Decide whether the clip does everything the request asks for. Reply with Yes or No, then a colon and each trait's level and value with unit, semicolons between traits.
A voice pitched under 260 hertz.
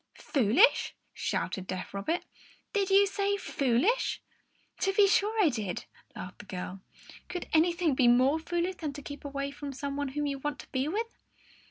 No: very high, 290 Hz